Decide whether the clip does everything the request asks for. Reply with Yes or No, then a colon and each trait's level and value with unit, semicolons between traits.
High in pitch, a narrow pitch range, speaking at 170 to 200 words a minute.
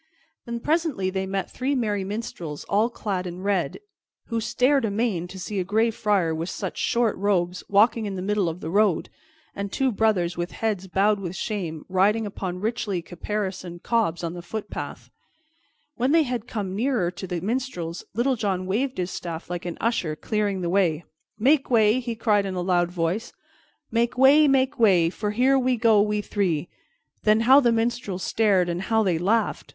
No: high, 205 Hz; average, 4.2 semitones; average, 185 wpm